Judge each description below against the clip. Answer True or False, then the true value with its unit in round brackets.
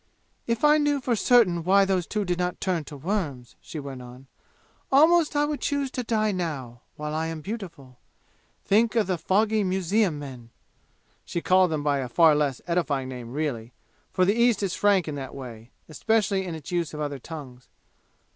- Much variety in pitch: True (6.8 semitones)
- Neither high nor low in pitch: True (175 Hz)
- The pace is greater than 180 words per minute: True (190 wpm)